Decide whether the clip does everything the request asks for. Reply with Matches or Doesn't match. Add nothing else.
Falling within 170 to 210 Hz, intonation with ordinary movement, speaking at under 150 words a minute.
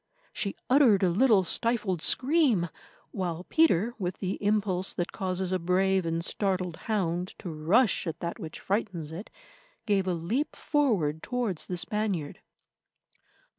Matches